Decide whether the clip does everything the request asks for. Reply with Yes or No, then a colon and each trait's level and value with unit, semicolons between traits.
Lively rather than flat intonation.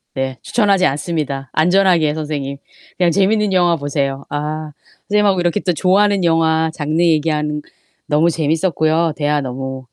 No: average, 3.3 semitones